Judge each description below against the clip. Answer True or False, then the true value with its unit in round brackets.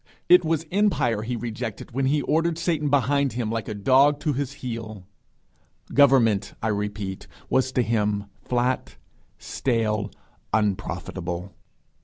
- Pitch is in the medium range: False (120 Hz)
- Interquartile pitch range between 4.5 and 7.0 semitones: True (4.9 semitones)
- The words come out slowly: True (130 wpm)